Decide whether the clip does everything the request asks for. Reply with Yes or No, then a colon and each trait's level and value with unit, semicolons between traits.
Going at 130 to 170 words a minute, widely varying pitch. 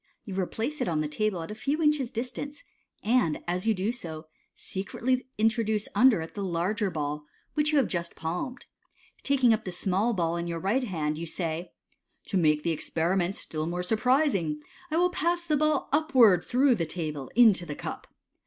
No: average, 190 wpm; wide, 7.0 semitones